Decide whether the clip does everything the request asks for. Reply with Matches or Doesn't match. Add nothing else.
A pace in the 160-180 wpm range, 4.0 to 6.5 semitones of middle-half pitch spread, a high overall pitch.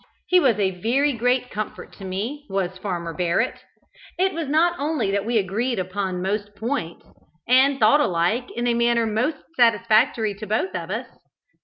Matches